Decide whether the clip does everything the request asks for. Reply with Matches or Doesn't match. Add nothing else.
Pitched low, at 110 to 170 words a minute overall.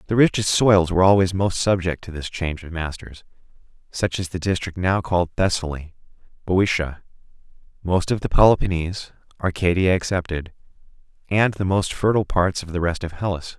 Matches